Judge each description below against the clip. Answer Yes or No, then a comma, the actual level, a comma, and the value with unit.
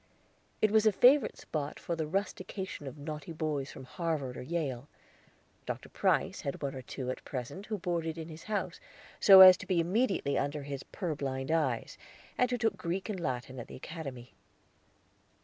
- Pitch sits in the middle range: Yes, medium, 160 Hz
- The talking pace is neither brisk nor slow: Yes, average, 180 wpm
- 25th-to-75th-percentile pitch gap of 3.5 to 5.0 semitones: No, wide, 5.5 semitones